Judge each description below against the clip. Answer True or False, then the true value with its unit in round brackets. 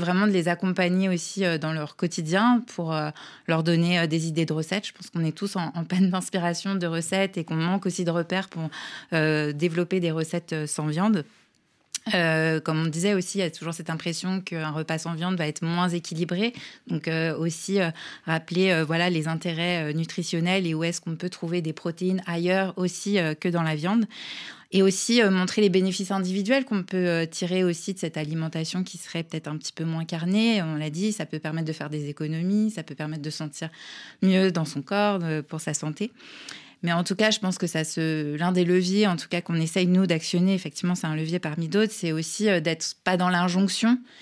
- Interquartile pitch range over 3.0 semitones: False (2.7 semitones)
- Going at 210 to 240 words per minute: True (215 wpm)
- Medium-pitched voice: True (175 Hz)